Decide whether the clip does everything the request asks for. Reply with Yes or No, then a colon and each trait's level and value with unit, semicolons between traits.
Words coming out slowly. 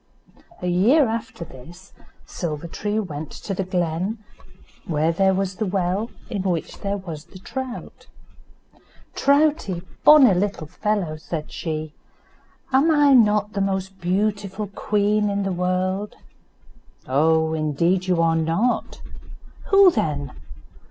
Yes: slow, 125 wpm